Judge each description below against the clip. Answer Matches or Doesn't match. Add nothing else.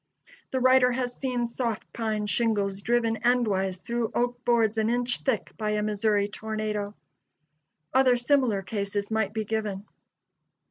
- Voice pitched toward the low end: Doesn't match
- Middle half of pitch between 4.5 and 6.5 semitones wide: Doesn't match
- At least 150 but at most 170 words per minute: Doesn't match